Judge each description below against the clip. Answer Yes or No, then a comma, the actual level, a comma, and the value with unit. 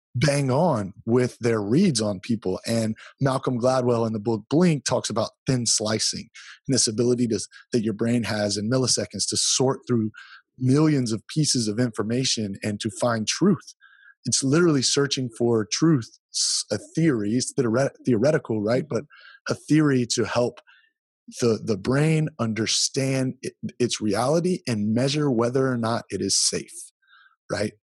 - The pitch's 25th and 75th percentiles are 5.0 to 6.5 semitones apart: No, average, 3.7 semitones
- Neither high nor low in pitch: No, low, 125 Hz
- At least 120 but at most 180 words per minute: Yes, average, 155 wpm